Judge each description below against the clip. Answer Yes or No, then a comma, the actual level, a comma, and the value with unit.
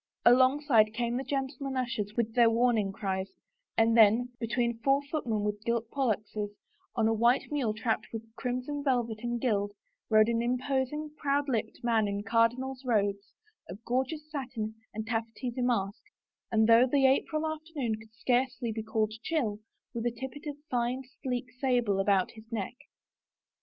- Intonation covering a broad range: No, average, 3.1 semitones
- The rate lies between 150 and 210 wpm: Yes, average, 155 wpm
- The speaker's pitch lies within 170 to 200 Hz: No, high, 235 Hz